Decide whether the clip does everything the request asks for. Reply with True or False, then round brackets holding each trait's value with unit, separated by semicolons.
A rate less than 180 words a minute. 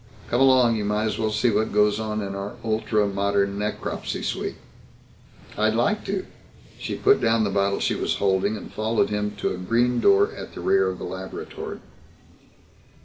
False (185 wpm)